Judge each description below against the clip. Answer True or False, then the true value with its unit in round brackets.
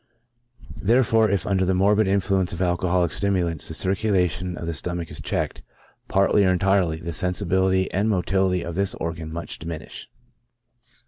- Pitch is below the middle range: True (95 Hz)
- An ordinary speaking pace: True (155 wpm)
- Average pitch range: False (2.3 semitones)